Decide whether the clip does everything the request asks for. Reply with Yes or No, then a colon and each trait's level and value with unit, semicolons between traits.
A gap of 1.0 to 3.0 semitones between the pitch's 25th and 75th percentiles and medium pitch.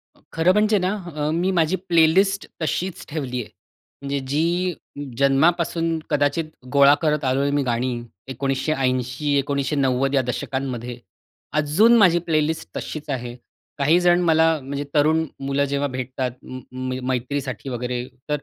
No: average, 3.7 semitones; medium, 145 Hz